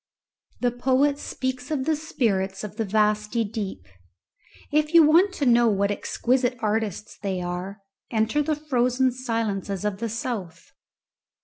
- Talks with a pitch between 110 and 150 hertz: No, high, 230 Hz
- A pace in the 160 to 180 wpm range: No, average, 140 wpm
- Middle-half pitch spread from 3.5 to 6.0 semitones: Yes, average, 4.2 semitones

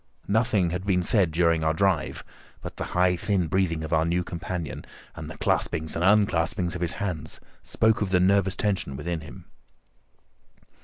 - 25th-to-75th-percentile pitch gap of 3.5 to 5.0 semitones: No, average, 3.0 semitones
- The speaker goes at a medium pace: Yes, average, 170 wpm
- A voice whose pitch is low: Yes, very low, 90 Hz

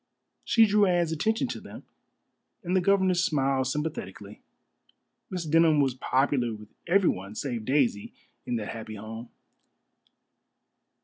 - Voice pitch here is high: No, medium, 145 Hz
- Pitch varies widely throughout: Yes, wide, 7.5 semitones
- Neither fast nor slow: No, slow, 125 wpm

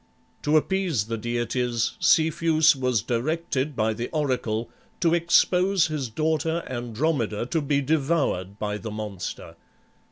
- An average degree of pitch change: No, wide, 5.8 semitones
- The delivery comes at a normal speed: No, slow, 125 wpm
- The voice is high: No, low, 135 Hz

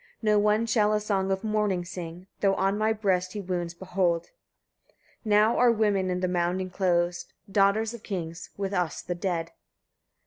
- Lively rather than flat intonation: No, average, 2.8 semitones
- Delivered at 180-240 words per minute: No, average, 170 wpm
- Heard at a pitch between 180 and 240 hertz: Yes, high, 190 Hz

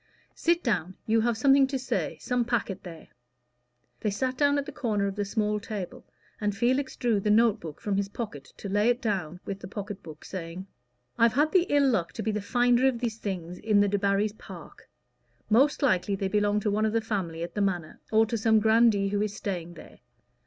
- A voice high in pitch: Yes, high, 210 Hz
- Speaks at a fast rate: Yes, fast, 215 wpm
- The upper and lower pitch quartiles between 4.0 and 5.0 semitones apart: No, average, 3.3 semitones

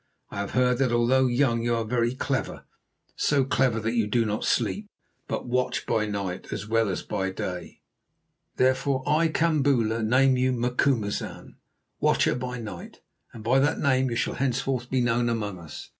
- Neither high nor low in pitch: No, low, 120 Hz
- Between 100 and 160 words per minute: No, average, 175 wpm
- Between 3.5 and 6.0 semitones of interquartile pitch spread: No, average, 2.8 semitones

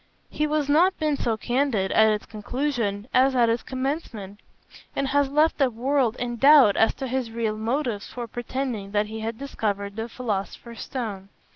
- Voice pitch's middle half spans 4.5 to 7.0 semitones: No, average, 4.0 semitones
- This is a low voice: No, high, 240 Hz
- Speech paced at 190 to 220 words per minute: No, average, 175 wpm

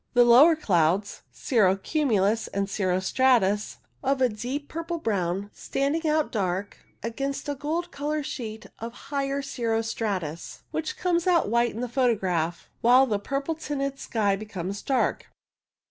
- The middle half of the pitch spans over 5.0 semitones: Yes, wide, 5.6 semitones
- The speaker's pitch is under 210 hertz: No, high, 235 Hz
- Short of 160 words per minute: Yes, average, 145 wpm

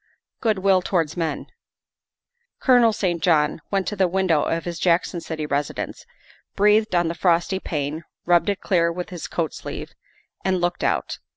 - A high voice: No, medium, 175 Hz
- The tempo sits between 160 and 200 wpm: Yes, average, 170 wpm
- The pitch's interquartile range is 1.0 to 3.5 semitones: Yes, narrow, 2.5 semitones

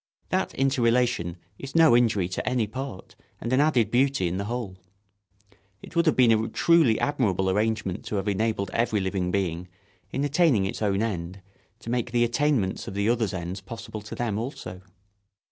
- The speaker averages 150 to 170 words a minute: No, average, 180 wpm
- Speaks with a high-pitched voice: No, low, 110 Hz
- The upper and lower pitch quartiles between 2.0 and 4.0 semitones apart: No, average, 4.5 semitones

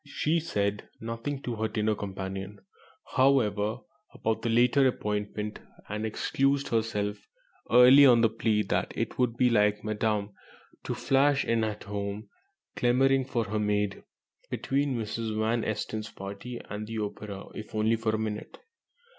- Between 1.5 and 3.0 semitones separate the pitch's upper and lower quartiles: Yes, average, 2.7 semitones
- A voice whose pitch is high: No, low, 110 Hz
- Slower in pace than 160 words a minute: Yes, average, 145 wpm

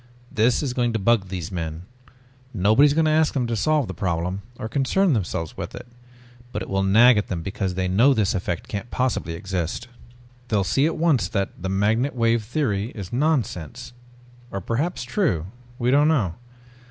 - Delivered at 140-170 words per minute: No, average, 190 wpm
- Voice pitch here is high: No, low, 110 Hz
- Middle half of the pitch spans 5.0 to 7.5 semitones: Yes, wide, 5.5 semitones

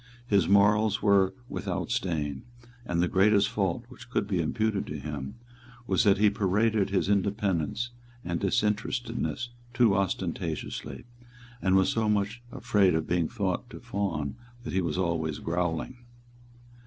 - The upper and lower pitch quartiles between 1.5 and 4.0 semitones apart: Yes, average, 3.5 semitones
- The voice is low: Yes, low, 100 Hz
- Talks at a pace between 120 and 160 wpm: Yes, average, 140 wpm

